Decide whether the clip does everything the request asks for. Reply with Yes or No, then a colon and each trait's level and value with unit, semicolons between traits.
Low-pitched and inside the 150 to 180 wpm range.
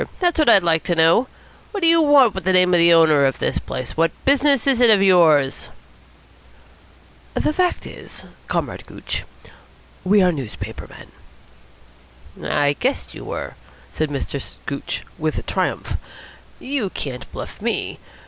No: medium, 180 Hz; average, 155 wpm